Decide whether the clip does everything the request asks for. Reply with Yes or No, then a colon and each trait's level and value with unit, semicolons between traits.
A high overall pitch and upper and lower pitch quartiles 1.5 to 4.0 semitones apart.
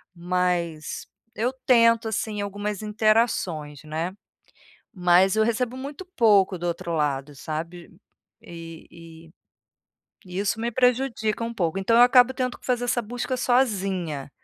No: high, 200 Hz; wide, 5.6 semitones